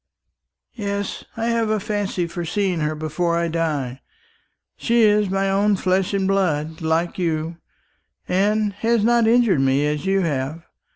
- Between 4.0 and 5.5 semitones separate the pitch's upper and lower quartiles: Yes, average, 4.5 semitones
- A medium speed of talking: Yes, average, 155 wpm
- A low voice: No, medium, 185 Hz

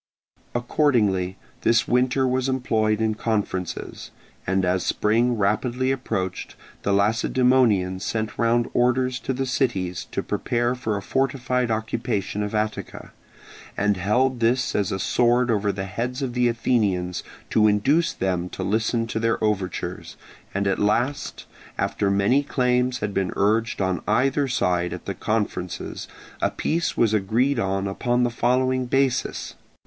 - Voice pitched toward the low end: Yes, low, 115 Hz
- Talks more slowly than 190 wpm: Yes, average, 145 wpm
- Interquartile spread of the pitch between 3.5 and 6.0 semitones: Yes, average, 3.9 semitones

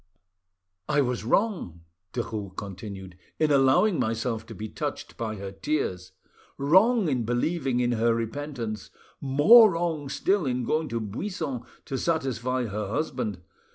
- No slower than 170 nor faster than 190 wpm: No, slow, 135 wpm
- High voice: No, low, 125 Hz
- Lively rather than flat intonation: Yes, wide, 5.9 semitones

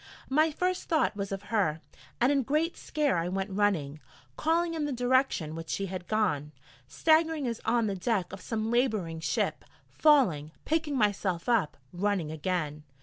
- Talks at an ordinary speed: Yes, average, 165 wpm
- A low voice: No, high, 210 Hz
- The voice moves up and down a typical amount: No, wide, 8.1 semitones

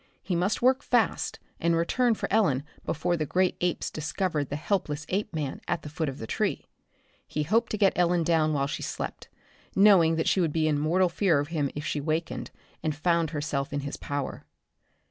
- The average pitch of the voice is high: No, medium, 165 Hz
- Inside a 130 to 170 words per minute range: No, average, 200 wpm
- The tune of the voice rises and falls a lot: No, average, 3.8 semitones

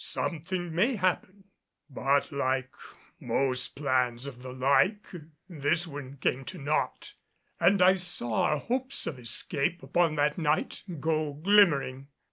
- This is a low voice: No, medium, 150 Hz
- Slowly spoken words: Yes, slow, 130 wpm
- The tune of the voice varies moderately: Yes, average, 4.9 semitones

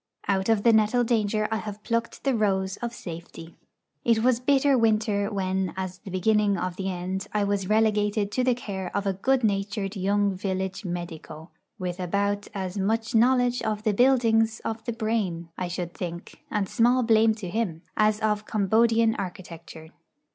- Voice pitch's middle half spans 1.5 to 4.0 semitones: Yes, average, 3.0 semitones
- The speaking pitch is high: Yes, high, 205 Hz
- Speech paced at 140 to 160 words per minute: No, average, 175 wpm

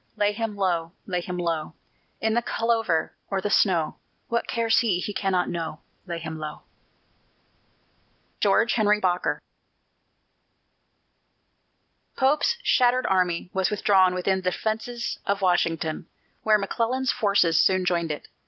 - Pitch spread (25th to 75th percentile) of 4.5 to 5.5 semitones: No, average, 4.1 semitones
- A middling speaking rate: No, slow, 130 wpm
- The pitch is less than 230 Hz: Yes, high, 190 Hz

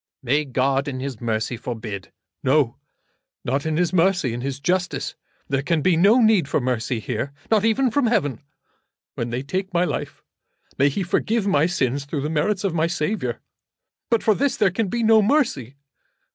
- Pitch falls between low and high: Yes, medium, 155 Hz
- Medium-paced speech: Yes, average, 185 wpm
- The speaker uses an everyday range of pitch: No, wide, 7.1 semitones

